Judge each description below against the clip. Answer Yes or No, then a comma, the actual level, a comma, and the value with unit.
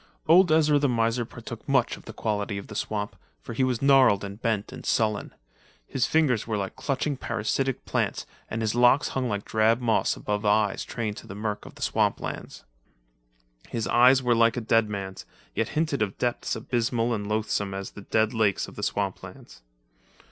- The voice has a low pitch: Yes, low, 115 Hz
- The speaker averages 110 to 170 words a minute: No, average, 190 wpm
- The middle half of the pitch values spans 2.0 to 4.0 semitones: Yes, average, 3.2 semitones